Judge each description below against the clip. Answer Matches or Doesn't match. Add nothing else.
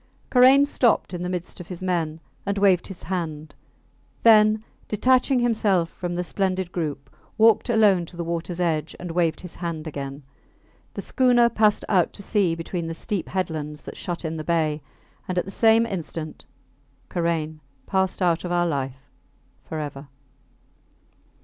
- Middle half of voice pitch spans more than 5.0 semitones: Doesn't match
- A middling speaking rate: Matches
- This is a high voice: Doesn't match